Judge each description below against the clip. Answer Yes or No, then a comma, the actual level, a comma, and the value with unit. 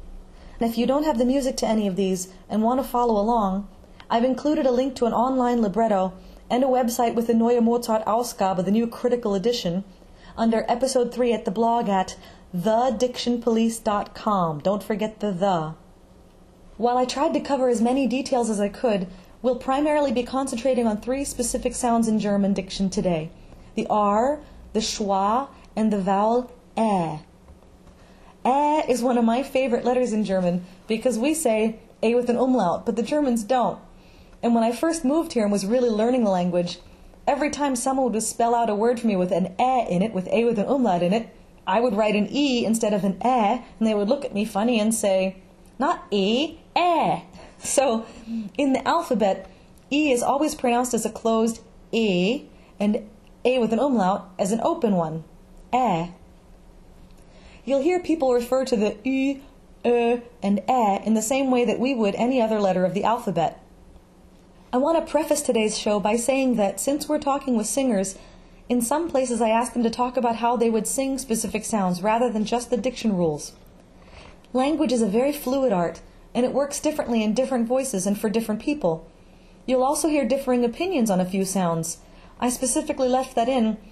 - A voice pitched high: Yes, high, 235 Hz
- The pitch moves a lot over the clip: No, average, 4.0 semitones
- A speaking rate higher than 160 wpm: Yes, average, 195 wpm